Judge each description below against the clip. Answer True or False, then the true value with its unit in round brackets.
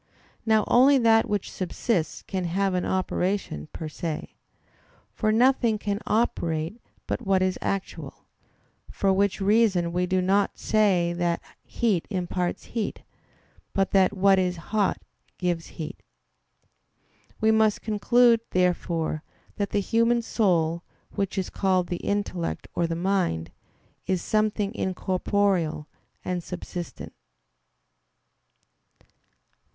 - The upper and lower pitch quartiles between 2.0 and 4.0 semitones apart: True (3.3 semitones)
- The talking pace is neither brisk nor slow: False (115 wpm)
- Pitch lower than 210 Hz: True (190 Hz)